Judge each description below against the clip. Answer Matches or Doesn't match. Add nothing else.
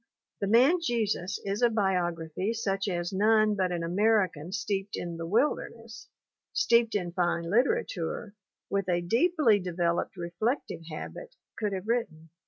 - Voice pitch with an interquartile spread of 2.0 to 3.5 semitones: Doesn't match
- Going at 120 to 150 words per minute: Matches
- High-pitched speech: Matches